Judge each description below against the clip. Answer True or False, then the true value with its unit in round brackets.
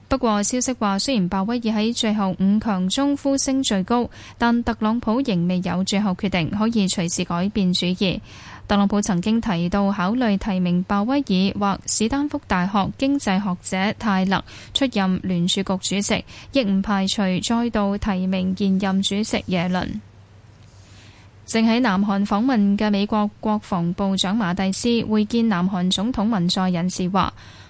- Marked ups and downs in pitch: False (2.9 semitones)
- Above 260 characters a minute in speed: False (245 characters per minute)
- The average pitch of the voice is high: True (200 Hz)